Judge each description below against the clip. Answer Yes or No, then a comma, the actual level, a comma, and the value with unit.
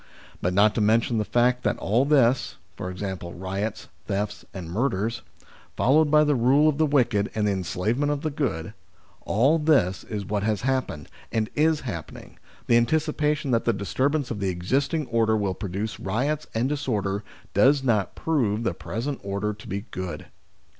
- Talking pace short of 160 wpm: No, average, 175 wpm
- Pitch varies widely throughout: Yes, wide, 5.7 semitones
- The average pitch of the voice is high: No, low, 115 Hz